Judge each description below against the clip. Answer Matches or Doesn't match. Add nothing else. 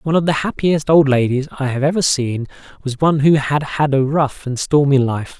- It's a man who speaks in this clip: Matches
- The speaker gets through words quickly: Matches